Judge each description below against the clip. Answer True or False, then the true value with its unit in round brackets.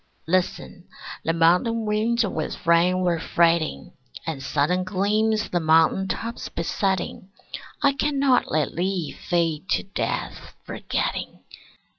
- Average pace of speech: False (115 wpm)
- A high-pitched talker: False (180 Hz)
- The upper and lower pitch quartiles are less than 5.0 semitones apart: True (4.2 semitones)